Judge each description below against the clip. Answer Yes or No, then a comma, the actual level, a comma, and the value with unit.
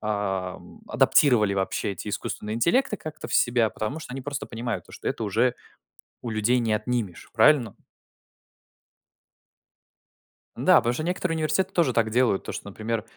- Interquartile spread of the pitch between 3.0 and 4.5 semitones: No, average, 4.9 semitones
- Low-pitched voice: Yes, low, 115 Hz